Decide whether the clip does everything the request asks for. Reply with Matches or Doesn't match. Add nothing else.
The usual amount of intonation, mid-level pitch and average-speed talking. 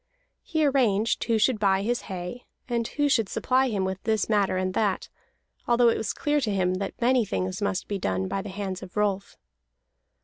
Doesn't match